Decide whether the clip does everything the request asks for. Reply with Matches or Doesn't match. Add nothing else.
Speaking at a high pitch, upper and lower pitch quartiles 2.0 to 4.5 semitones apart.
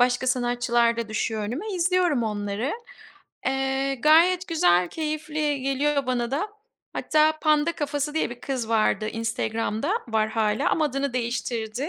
Doesn't match